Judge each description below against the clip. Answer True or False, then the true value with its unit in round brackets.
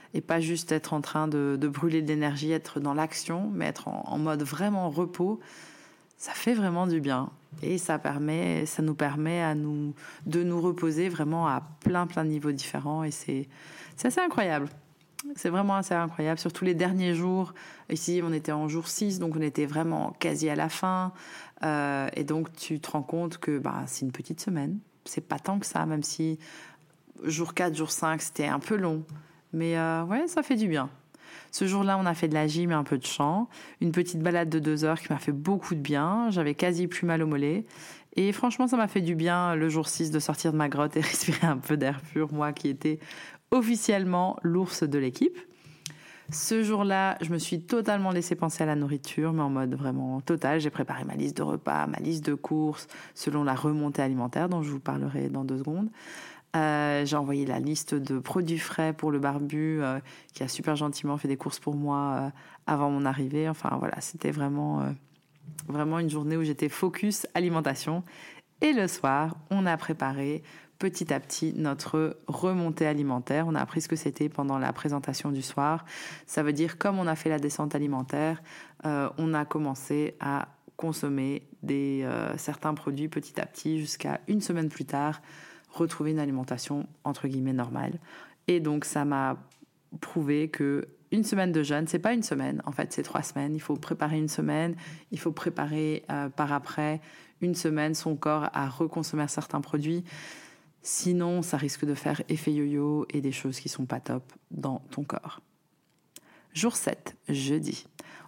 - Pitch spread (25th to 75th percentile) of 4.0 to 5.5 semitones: False (2.6 semitones)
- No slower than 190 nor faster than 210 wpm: True (195 wpm)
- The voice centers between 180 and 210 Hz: False (155 Hz)